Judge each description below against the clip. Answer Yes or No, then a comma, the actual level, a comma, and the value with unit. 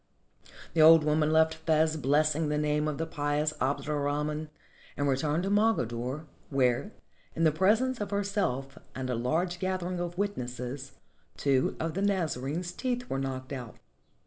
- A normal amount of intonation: Yes, average, 4.3 semitones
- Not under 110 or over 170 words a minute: Yes, average, 160 wpm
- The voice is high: No, medium, 155 Hz